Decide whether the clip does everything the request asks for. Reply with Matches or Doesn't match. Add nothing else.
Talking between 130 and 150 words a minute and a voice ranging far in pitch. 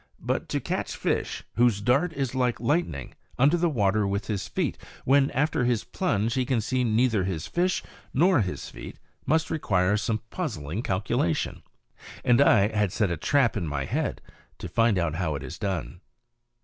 Doesn't match